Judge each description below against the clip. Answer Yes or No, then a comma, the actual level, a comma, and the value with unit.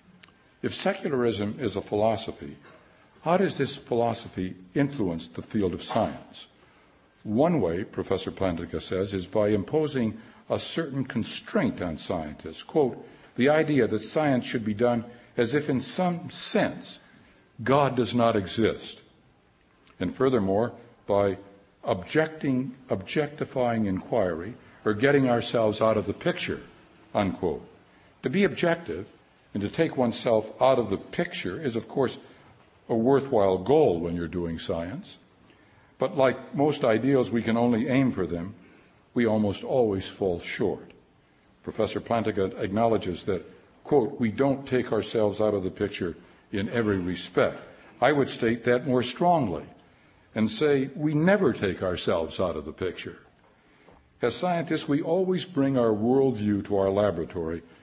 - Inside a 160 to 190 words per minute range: No, average, 140 wpm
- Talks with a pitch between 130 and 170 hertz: No, low, 115 Hz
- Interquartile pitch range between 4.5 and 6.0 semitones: Yes, average, 5.2 semitones